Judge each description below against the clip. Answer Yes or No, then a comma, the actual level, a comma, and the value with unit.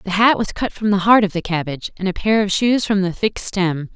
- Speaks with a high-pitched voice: Yes, high, 195 Hz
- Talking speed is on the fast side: Yes, fast, 290 wpm